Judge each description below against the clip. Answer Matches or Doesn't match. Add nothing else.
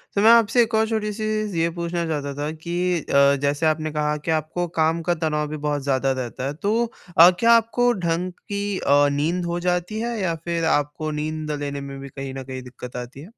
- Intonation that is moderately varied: Matches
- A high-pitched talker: Doesn't match